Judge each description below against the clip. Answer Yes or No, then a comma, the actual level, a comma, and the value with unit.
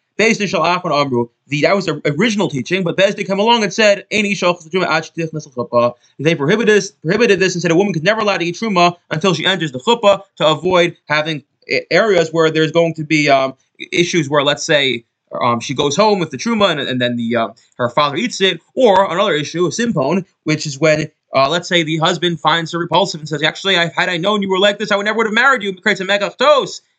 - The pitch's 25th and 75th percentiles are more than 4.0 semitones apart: Yes, average, 4.6 semitones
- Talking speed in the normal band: No, fast, 220 wpm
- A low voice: No, medium, 175 Hz